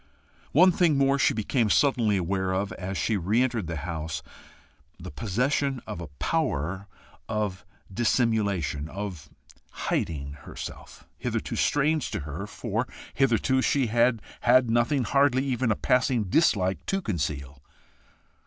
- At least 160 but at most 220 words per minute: No, slow, 135 wpm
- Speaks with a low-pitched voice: Yes, low, 110 Hz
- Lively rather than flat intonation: Yes, wide, 6.1 semitones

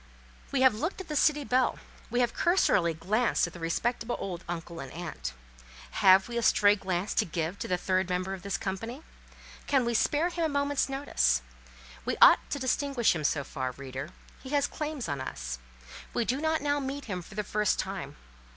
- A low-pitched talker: No, high, 210 Hz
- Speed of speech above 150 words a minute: Yes, average, 200 wpm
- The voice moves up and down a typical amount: No, wide, 7.9 semitones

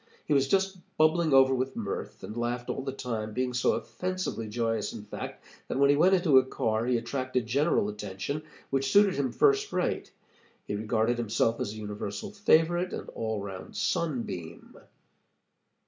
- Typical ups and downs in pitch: No, wide, 5.9 semitones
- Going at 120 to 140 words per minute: No, average, 170 wpm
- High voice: No, low, 125 Hz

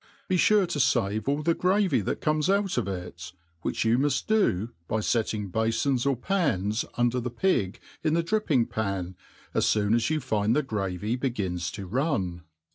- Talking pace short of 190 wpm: Yes, average, 170 wpm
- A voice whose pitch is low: Yes, low, 120 Hz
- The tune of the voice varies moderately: No, wide, 7.0 semitones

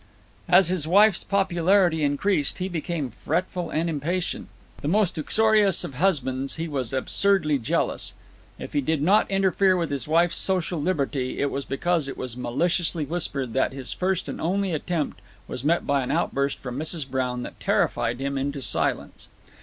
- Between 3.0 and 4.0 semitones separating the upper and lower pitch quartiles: No, average, 4.8 semitones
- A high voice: No, medium, 160 Hz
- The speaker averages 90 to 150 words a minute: No, average, 170 wpm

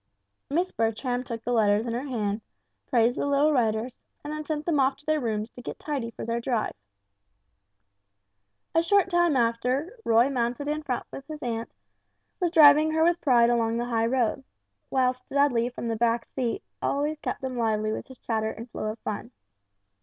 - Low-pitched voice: No, high, 245 Hz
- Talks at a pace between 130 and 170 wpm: No, average, 185 wpm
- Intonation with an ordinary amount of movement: Yes, average, 4.1 semitones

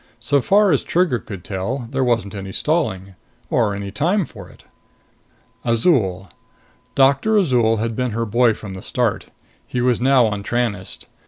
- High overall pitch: No, low, 120 Hz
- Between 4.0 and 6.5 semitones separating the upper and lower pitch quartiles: Yes, average, 4.9 semitones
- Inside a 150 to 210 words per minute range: Yes, average, 160 wpm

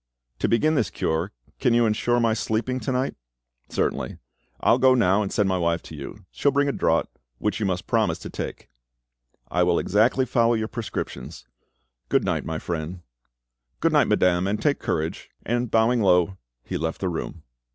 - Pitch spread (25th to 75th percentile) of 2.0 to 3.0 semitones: No, wide, 5.4 semitones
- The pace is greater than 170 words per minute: Yes, average, 185 wpm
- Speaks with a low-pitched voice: Yes, low, 105 Hz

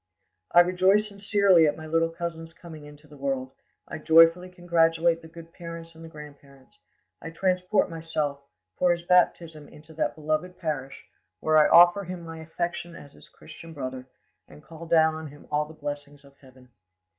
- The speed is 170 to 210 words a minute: Yes, average, 175 wpm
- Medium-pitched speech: Yes, medium, 165 Hz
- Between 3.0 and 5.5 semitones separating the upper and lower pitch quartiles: No, narrow, 2.6 semitones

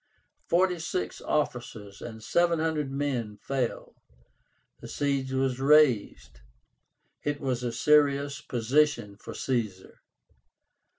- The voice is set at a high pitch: No, low, 135 Hz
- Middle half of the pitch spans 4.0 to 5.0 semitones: Yes, average, 4.3 semitones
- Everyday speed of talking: No, slow, 105 wpm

